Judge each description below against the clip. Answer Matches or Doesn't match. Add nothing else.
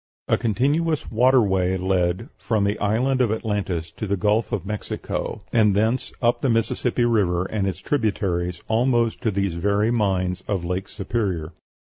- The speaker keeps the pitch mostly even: Doesn't match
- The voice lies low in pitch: Matches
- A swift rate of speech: Doesn't match